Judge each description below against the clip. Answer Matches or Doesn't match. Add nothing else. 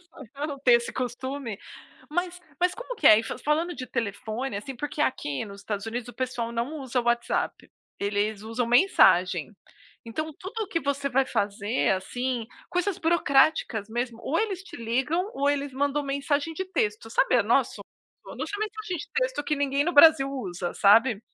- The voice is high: Matches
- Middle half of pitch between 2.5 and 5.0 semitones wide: Doesn't match